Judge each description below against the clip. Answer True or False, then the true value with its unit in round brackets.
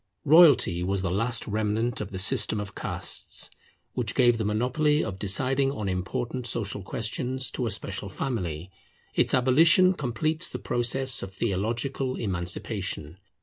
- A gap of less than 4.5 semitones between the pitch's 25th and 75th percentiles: False (5.1 semitones)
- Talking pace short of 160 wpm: True (145 wpm)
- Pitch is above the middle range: False (115 Hz)